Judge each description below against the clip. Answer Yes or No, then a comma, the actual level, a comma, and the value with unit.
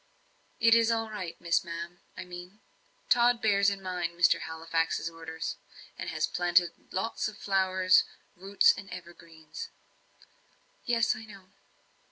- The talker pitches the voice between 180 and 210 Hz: Yes, medium, 185 Hz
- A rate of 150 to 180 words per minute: No, slow, 135 wpm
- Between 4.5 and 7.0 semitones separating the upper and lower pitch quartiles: No, average, 3.4 semitones